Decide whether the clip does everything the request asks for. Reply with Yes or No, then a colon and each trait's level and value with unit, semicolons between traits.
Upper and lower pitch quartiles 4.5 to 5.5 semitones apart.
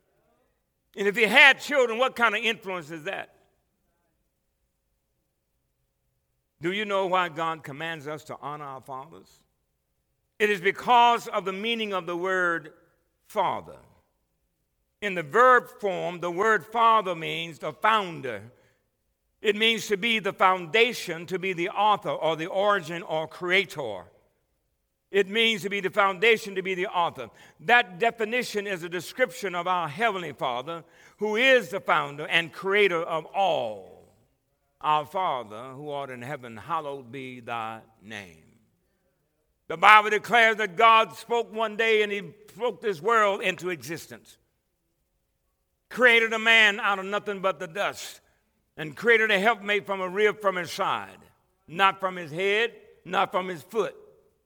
Yes: average, 5.2 semitones